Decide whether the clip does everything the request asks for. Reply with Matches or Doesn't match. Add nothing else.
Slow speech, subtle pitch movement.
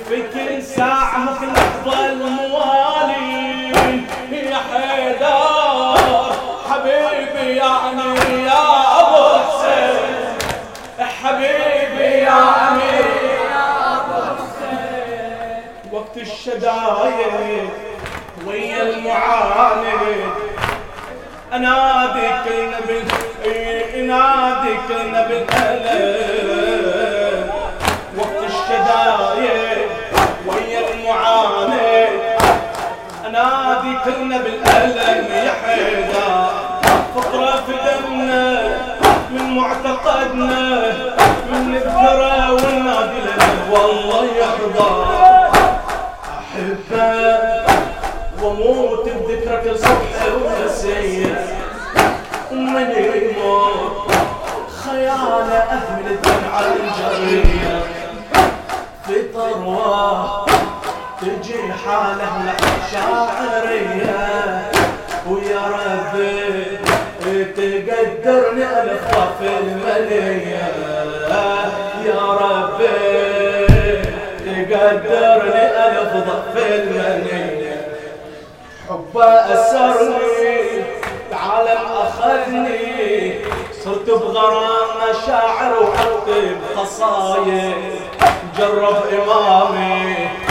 Doesn't match